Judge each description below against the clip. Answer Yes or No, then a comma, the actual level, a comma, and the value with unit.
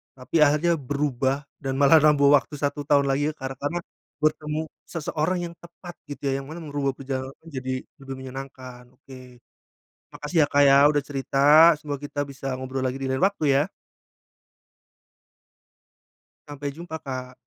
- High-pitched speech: No, medium, 140 Hz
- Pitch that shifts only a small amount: Yes, narrow, 2.2 semitones